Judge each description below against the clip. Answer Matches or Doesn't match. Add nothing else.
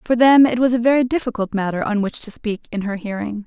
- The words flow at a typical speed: Doesn't match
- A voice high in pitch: Matches